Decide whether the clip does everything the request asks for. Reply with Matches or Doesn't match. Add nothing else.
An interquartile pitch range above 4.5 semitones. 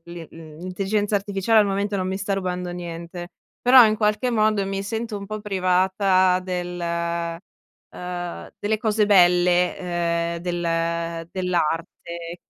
Doesn't match